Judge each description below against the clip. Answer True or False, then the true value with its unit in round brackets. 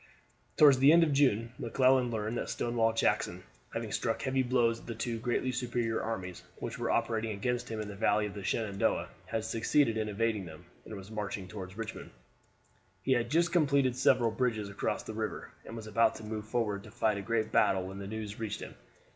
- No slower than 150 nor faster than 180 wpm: False (205 wpm)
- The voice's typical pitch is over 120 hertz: False (115 Hz)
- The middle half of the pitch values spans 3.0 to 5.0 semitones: False (2.5 semitones)